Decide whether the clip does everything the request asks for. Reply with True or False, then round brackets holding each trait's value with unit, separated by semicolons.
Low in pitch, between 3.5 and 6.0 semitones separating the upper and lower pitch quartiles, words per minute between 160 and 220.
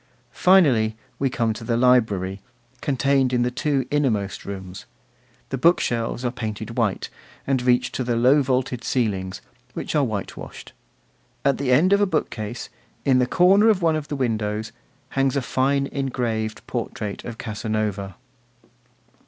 False (125 Hz; 4.0 semitones; 150 wpm)